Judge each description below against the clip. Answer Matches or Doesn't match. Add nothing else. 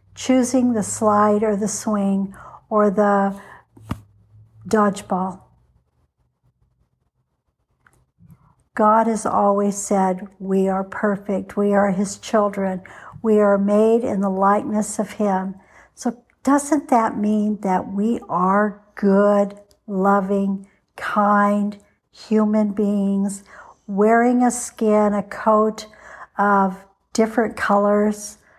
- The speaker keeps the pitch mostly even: Matches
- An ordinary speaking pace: Doesn't match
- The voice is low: Doesn't match